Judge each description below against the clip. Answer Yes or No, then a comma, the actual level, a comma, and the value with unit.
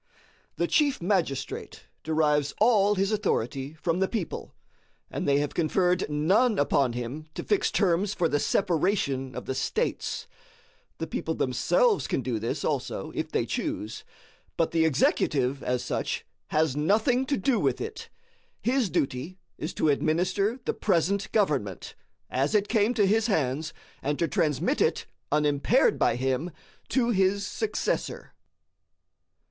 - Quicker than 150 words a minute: No, average, 145 wpm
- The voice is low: No, medium, 165 Hz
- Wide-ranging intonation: Yes, wide, 6.5 semitones